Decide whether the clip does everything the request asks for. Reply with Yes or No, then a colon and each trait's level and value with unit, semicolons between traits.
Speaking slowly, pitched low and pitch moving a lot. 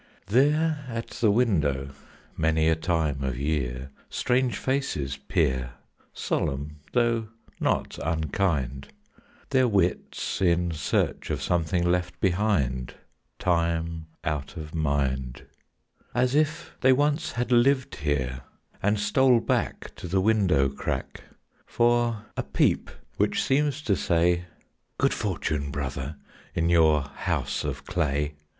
Yes: slow, 120 wpm; very low, 85 Hz; wide, 8.4 semitones